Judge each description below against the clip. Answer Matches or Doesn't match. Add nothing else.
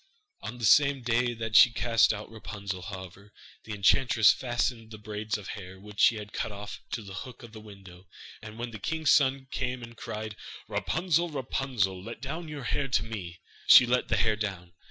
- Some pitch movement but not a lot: Matches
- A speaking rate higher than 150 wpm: Matches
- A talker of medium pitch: Doesn't match